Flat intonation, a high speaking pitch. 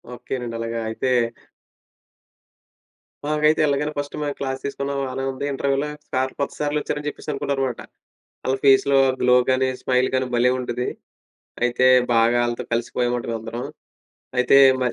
No: narrow, 2.3 semitones; low, 130 Hz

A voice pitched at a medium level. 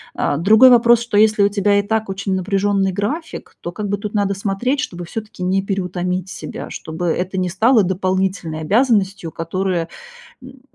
No: high, 195 Hz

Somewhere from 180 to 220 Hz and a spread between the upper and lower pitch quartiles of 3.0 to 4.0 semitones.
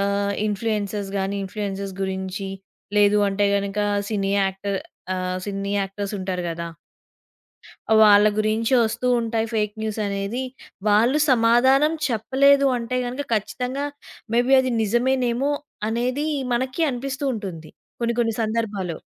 Yes: high, 215 Hz; average, 3.5 semitones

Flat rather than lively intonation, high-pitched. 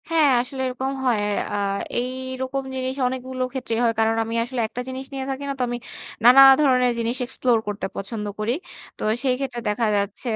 Yes: narrow, 2.3 semitones; very high, 250 Hz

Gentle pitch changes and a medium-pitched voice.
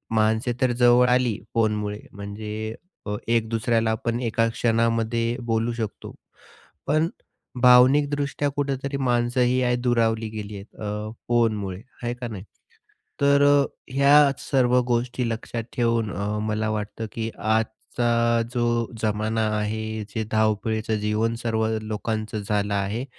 No: narrow, 2.1 semitones; low, 115 Hz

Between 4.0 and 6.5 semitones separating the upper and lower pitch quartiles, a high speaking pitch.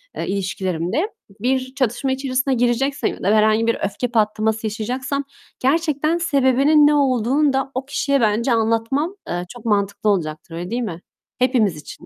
Yes: average, 4.3 semitones; high, 245 Hz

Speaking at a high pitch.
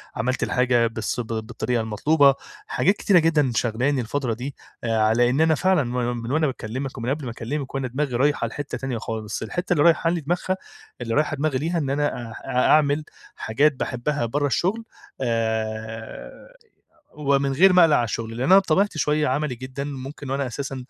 No: low, 135 Hz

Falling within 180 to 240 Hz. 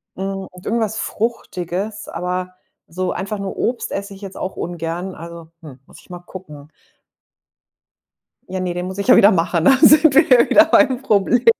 Yes: high, 190 Hz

